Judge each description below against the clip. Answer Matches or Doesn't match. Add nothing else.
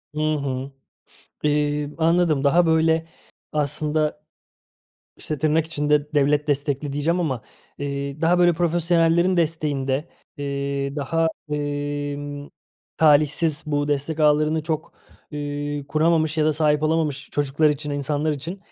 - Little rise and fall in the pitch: Matches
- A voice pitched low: Doesn't match